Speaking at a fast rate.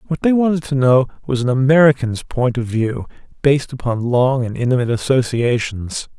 No: average, 165 wpm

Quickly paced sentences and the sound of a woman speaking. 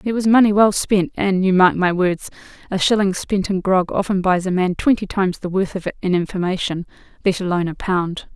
Yes: fast, 225 wpm; female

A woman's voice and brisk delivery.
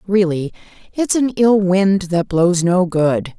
No: female; average, 160 wpm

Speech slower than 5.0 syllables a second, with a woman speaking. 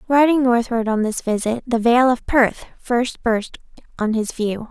Yes: 4.3 syllables/s; female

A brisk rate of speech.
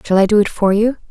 Yes: fast, 325 wpm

